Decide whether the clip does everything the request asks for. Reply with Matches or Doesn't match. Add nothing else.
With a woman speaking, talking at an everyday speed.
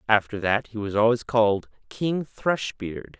Doesn't match